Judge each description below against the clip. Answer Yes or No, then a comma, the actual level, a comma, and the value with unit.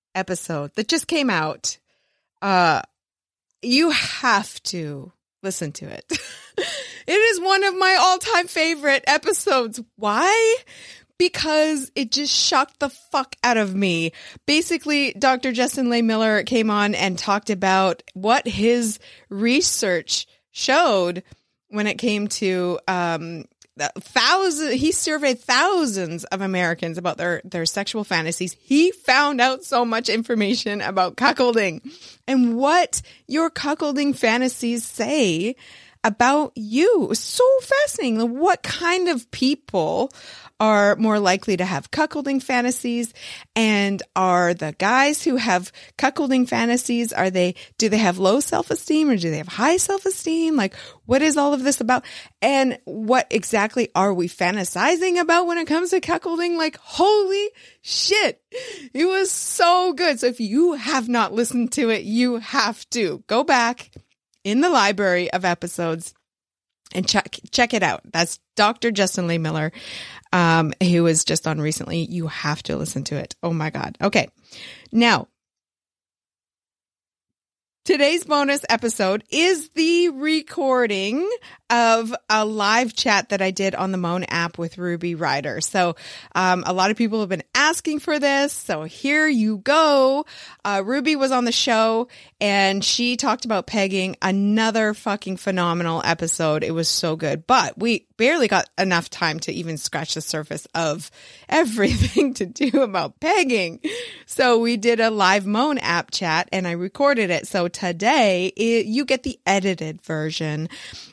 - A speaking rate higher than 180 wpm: No, average, 150 wpm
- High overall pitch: Yes, high, 225 Hz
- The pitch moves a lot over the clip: Yes, wide, 7.6 semitones